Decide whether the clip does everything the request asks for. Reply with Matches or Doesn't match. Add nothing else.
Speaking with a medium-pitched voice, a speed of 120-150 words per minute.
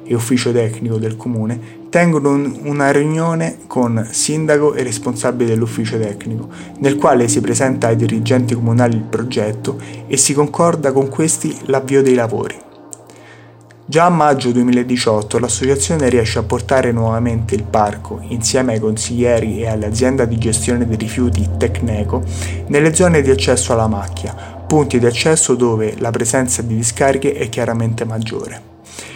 Doesn't match